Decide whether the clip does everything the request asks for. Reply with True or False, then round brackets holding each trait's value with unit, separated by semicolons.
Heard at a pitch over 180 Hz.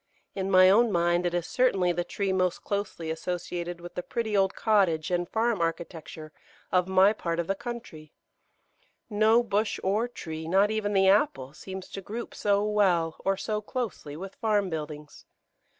True (190 Hz)